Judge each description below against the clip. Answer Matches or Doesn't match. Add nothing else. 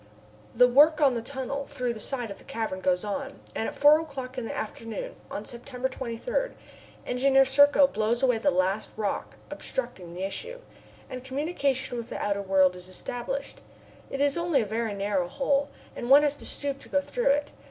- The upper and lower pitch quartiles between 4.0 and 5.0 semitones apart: Matches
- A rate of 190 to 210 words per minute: Matches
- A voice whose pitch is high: Matches